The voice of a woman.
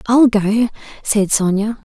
Yes: female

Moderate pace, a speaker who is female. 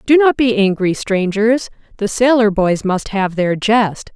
Yes: average, 175 wpm; female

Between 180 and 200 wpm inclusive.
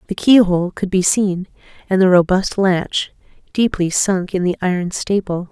No: average, 165 wpm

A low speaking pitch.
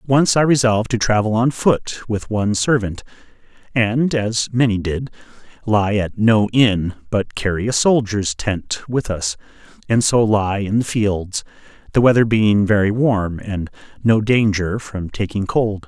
Yes: low, 110 Hz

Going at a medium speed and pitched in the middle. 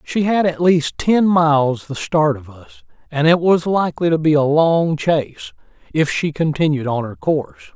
Yes: average, 195 wpm; medium, 150 Hz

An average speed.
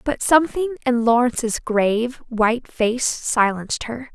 No: slow, 130 wpm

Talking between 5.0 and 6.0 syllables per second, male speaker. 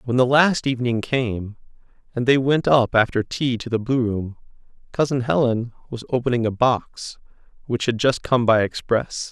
No: 4.7 syllables/s; male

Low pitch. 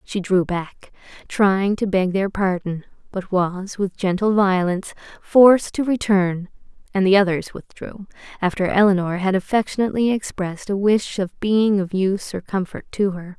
No: high, 195 Hz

